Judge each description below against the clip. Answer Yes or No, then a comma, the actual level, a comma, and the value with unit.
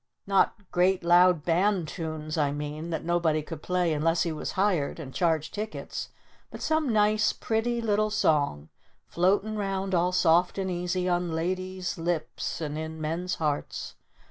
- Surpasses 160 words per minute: No, average, 155 wpm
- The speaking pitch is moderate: Yes, medium, 175 Hz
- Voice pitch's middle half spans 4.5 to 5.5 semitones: No, average, 3.2 semitones